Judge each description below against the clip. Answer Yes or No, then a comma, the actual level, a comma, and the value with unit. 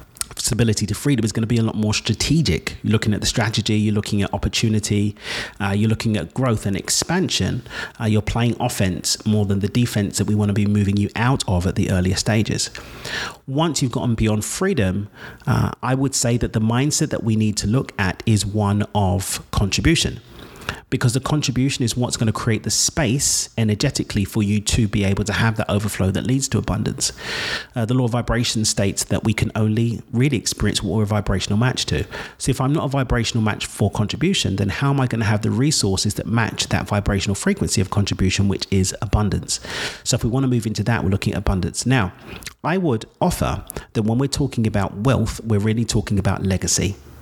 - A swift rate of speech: Yes, fast, 210 wpm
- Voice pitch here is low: Yes, low, 110 Hz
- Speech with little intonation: No, average, 3.1 semitones